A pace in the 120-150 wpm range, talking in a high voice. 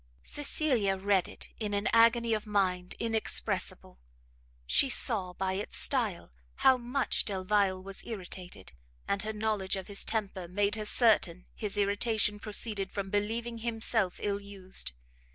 Yes: average, 140 wpm; high, 205 Hz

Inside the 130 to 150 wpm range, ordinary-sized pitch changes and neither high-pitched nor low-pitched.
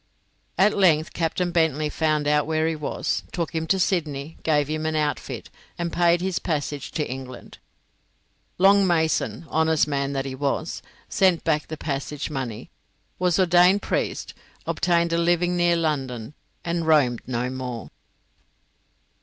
Yes: average, 145 wpm; average, 3.0 semitones; medium, 160 Hz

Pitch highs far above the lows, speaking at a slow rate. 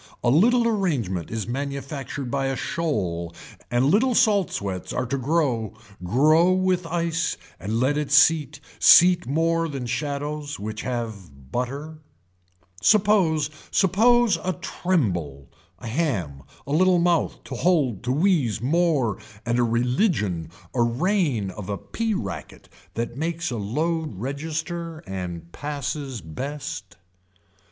Yes: wide, 6.9 semitones; slow, 130 wpm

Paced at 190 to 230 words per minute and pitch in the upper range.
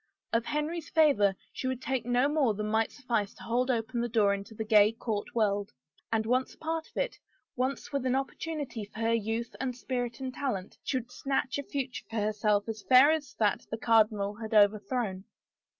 Yes: average, 200 wpm; high, 235 Hz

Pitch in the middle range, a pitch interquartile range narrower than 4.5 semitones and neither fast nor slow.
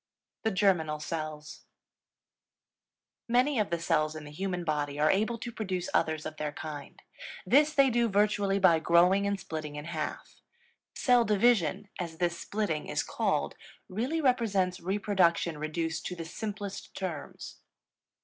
No: medium, 180 Hz; average, 5.0 semitones; average, 145 wpm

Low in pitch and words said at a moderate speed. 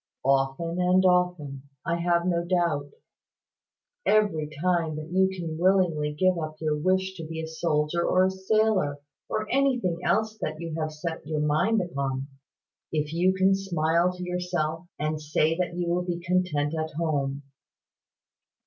No: medium, 170 Hz; average, 160 wpm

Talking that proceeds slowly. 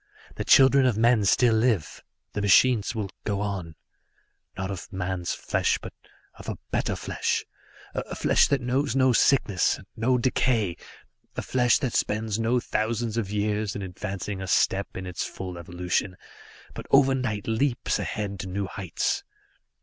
No: average, 155 wpm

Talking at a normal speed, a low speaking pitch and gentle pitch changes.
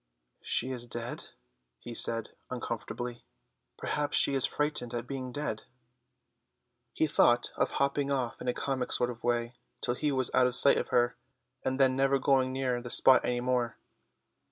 Yes: average, 170 wpm; low, 125 Hz; narrow, 2.0 semitones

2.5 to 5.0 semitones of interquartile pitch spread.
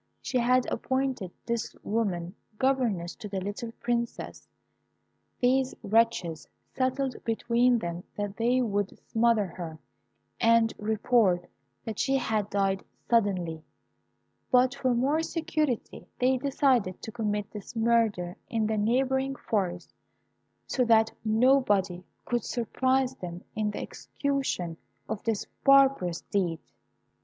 Yes: average, 4.2 semitones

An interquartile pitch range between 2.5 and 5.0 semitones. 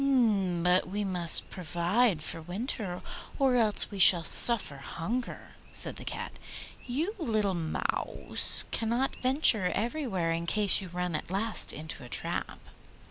No: wide, 5.4 semitones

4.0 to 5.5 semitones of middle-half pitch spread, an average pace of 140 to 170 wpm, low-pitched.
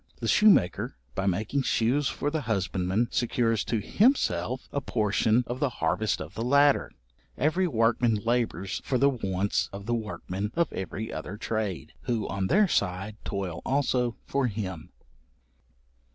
Yes: average, 5.0 semitones; average, 150 wpm; low, 110 Hz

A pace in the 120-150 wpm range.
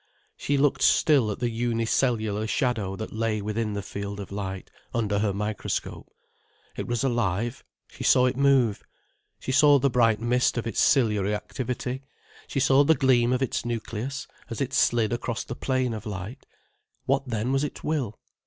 No: average, 170 wpm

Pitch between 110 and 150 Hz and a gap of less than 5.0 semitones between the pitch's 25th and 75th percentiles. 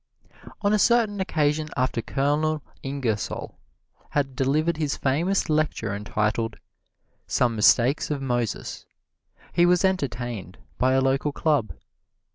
Yes: medium, 140 Hz; average, 4.4 semitones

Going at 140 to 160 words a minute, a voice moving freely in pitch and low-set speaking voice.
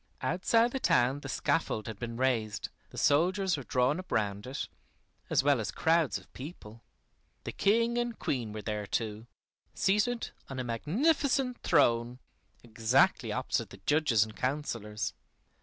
Yes: average, 150 wpm; wide, 8.4 semitones; low, 130 Hz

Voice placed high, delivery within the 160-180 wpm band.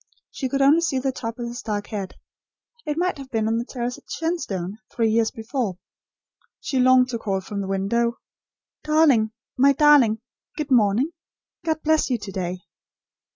Yes: high, 240 Hz; average, 175 wpm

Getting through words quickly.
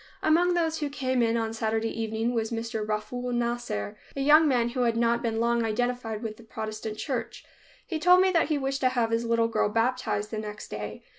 Yes: fast, 215 wpm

